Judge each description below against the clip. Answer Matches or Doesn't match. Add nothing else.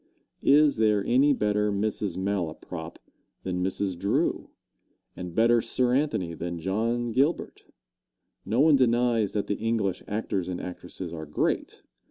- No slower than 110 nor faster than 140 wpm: Matches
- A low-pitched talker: Matches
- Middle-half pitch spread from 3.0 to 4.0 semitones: Doesn't match